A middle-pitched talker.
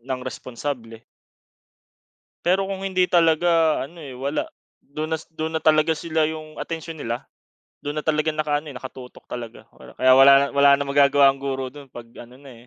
Yes: medium, 145 Hz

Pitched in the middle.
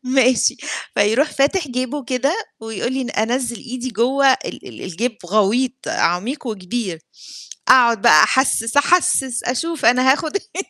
No: very high, 255 Hz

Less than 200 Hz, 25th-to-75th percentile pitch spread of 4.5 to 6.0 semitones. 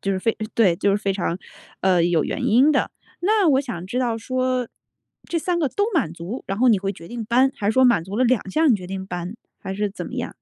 No: high, 220 Hz; average, 5.2 semitones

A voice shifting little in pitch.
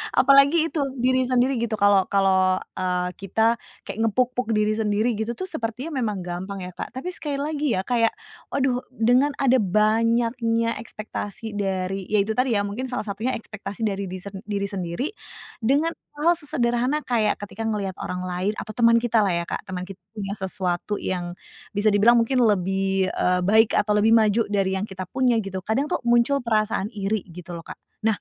No: average, 3.9 semitones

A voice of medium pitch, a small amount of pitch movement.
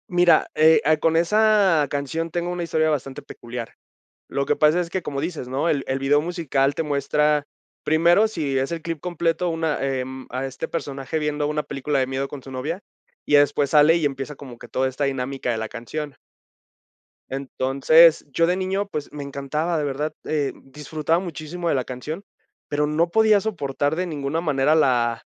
No: medium, 150 Hz; average, 3.4 semitones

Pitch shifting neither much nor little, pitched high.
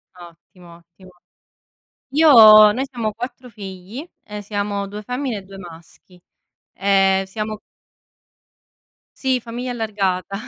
Yes: average, 4.0 semitones; high, 205 Hz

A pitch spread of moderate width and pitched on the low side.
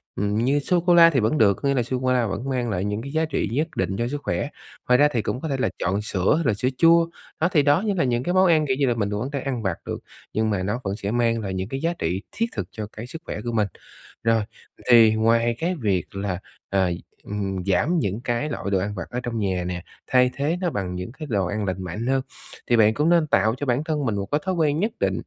No: wide, 6.1 semitones; low, 120 Hz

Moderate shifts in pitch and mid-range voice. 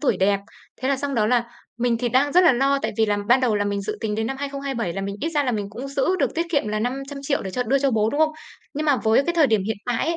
No: average, 4.2 semitones; very high, 255 Hz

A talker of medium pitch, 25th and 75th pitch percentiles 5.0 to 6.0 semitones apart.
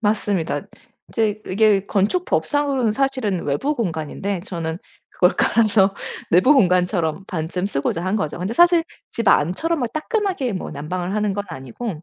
No: high, 200 Hz; average, 5.3 semitones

